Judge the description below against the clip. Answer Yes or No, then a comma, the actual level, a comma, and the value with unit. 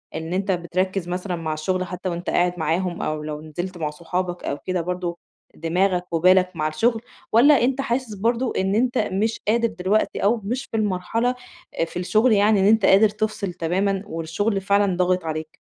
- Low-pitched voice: No, medium, 185 Hz